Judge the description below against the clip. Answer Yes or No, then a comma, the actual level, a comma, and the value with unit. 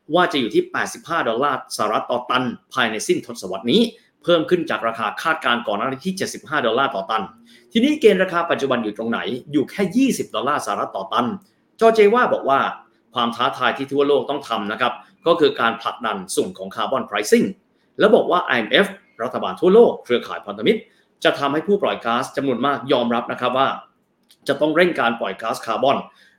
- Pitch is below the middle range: No, medium, 150 Hz